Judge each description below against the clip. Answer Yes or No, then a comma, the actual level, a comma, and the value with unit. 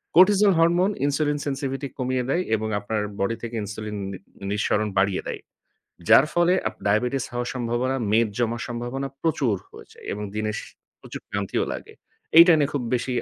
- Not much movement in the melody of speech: No, average, 5.0 semitones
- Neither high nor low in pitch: No, low, 125 Hz